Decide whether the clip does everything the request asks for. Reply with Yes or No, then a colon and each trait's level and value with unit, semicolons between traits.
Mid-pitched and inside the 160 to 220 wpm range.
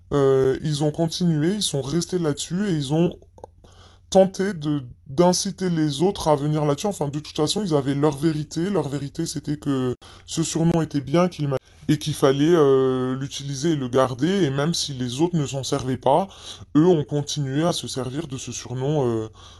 Yes: medium, 145 Hz; average, 195 wpm